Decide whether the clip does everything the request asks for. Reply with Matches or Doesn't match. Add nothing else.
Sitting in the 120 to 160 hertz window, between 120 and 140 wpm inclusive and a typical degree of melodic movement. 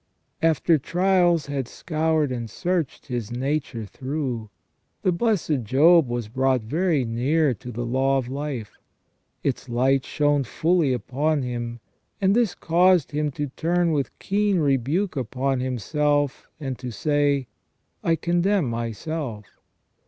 Matches